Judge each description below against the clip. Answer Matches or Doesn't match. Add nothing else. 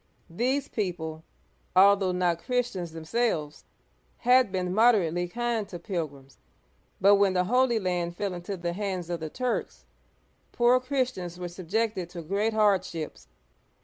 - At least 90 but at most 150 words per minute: Matches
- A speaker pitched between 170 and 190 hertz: Matches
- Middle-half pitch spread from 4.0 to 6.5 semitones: Matches